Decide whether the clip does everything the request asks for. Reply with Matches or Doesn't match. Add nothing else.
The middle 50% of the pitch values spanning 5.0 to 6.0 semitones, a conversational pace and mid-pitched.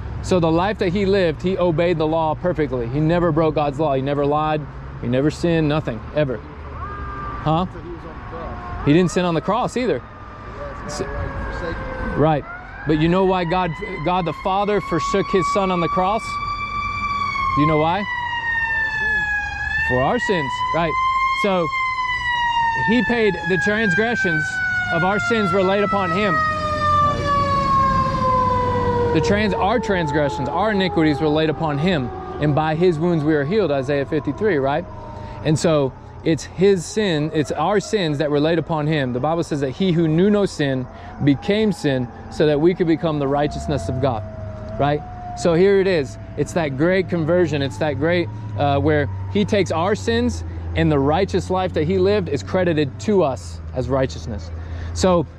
Matches